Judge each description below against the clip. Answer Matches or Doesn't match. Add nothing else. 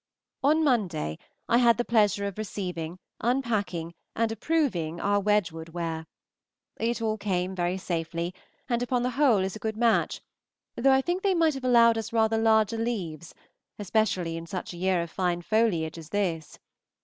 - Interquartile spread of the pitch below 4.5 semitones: Doesn't match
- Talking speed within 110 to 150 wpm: Doesn't match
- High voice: Matches